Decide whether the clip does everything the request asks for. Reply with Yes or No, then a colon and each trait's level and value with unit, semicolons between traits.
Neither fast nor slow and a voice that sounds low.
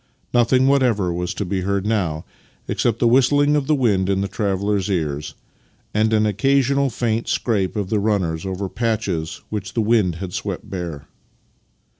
Yes: average, 165 wpm; low, 105 Hz